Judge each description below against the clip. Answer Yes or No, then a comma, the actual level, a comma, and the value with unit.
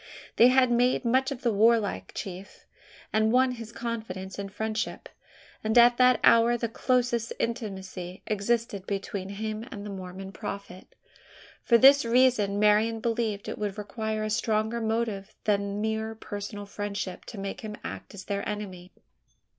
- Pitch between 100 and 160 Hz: No, high, 215 Hz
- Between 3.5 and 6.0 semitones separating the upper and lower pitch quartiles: No, average, 2.7 semitones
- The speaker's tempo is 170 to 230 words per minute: No, average, 155 wpm